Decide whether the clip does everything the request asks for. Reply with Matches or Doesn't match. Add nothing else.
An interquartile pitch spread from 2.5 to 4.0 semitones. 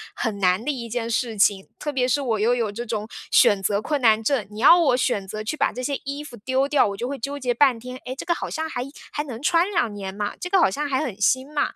Doesn't match